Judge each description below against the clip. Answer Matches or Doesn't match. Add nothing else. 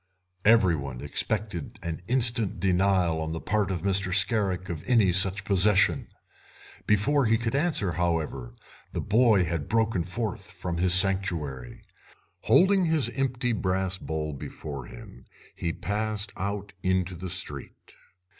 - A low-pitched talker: Matches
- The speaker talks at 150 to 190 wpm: Doesn't match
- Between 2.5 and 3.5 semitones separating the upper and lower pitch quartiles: Doesn't match